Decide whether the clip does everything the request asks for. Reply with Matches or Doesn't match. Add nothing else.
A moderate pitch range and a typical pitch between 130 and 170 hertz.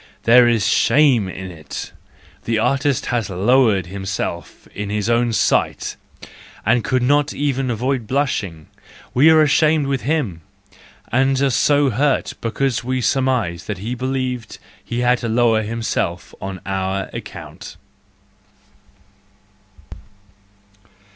Doesn't match